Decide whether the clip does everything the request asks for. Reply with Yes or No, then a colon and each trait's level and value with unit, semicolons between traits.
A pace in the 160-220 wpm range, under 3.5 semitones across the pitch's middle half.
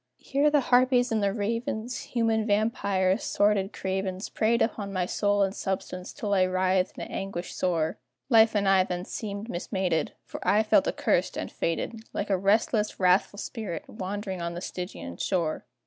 Yes: average, 165 wpm; average, 2.9 semitones